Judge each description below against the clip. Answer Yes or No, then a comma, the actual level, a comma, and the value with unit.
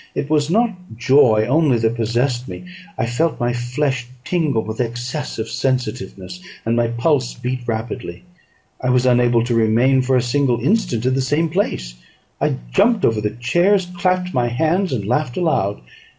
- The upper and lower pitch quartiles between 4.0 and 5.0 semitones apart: Yes, average, 4.7 semitones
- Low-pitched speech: Yes, low, 125 Hz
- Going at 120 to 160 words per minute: No, average, 170 wpm